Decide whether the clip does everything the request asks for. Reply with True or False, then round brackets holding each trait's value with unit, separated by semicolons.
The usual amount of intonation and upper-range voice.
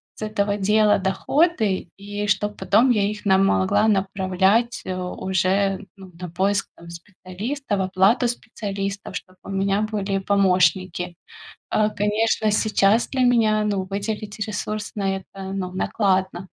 False (2.0 semitones; 200 Hz)